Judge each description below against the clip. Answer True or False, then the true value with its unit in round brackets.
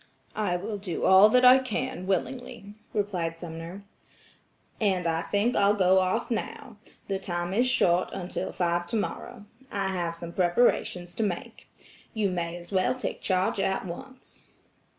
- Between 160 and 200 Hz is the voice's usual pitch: True (190 Hz)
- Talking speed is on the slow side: False (150 wpm)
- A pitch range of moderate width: True (3.7 semitones)